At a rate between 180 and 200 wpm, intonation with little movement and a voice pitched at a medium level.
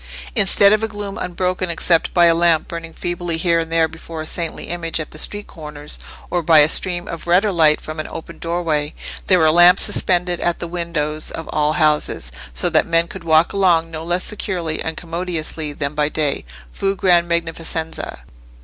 Yes: average, 190 wpm; narrow, 2.0 semitones; medium, 165 Hz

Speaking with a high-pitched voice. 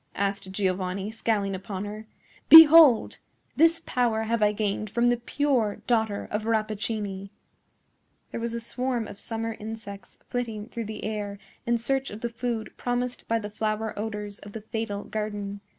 Yes: high, 220 Hz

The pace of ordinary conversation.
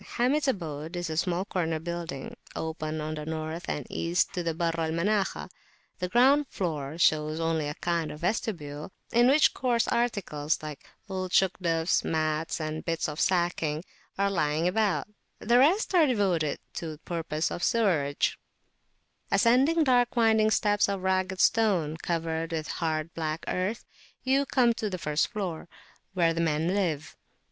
Yes: average, 155 wpm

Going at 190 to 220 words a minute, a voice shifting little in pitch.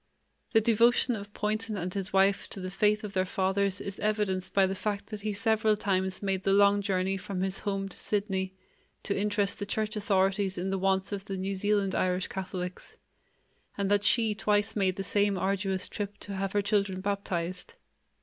Yes: average, 195 wpm; narrow, 1.5 semitones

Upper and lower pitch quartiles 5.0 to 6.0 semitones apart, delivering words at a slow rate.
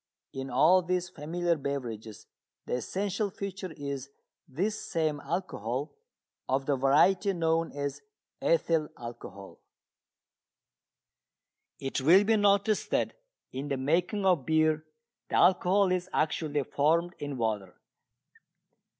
Yes: average, 5.3 semitones; slow, 115 wpm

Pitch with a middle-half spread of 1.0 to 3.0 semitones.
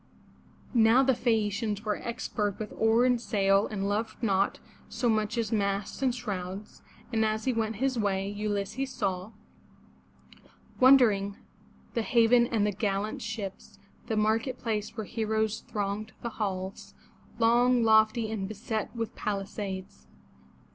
Yes: narrow, 2.4 semitones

